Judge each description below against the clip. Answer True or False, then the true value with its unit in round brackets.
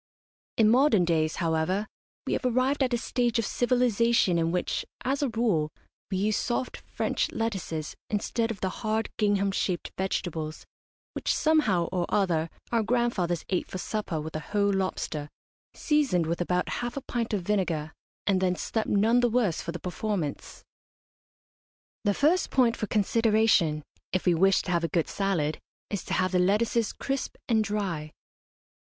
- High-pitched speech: True (200 Hz)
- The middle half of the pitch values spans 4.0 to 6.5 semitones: True (4.9 semitones)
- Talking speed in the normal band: True (165 wpm)